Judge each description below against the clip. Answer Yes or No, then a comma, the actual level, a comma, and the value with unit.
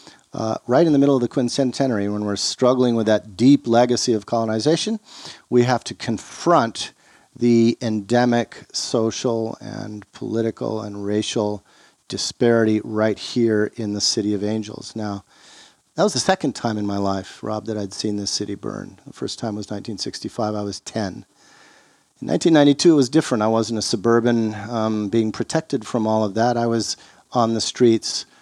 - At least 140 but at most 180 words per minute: Yes, average, 170 wpm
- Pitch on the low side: Yes, low, 115 Hz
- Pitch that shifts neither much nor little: No, narrow, 2.3 semitones